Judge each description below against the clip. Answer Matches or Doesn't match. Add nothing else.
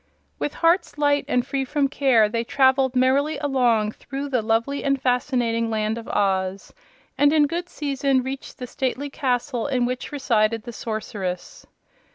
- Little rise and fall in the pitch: Doesn't match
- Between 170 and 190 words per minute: Doesn't match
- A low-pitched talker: Doesn't match